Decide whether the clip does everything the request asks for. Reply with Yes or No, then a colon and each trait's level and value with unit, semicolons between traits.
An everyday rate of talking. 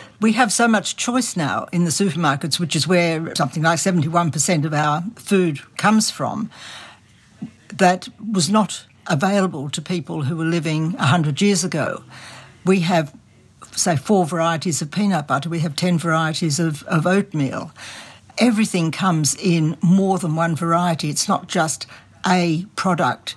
Yes: average, 150 wpm